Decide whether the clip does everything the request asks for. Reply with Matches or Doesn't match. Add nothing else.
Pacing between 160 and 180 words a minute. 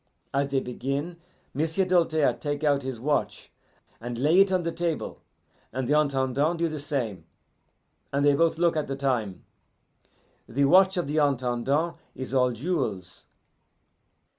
Doesn't match